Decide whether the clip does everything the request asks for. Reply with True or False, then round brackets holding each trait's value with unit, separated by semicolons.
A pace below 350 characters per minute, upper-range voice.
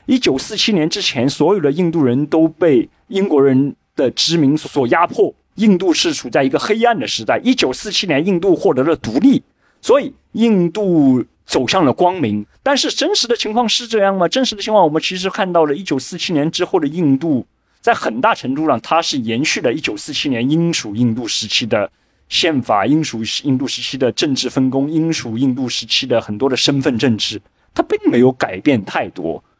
False (300 characters per minute; 170 Hz)